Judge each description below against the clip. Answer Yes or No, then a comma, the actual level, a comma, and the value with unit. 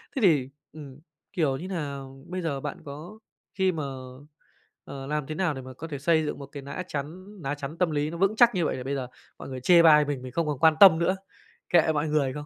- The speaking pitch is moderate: Yes, medium, 150 Hz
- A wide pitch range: No, average, 3.5 semitones